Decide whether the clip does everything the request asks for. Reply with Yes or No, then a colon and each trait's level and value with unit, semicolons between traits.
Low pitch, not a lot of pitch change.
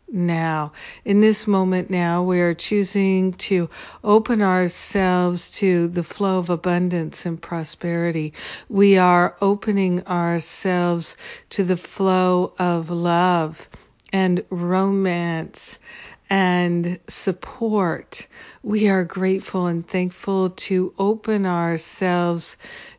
No: medium, 180 Hz; narrow, 2.0 semitones